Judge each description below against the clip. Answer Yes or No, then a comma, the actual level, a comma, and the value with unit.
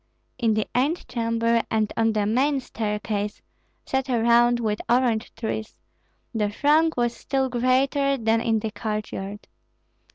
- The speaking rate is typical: No, slow, 130 wpm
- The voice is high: Yes, high, 230 Hz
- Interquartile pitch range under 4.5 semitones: Yes, average, 2.8 semitones